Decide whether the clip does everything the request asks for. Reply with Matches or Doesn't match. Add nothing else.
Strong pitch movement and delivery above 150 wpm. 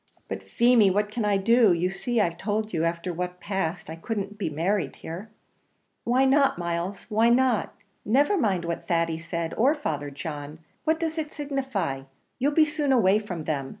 Matches